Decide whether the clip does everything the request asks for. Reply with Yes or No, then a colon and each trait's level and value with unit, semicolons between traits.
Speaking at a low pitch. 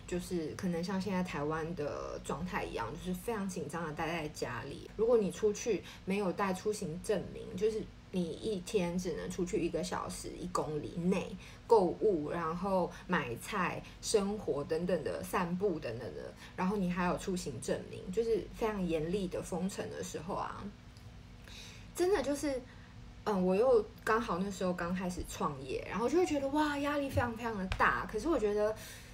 No: high, 195 Hz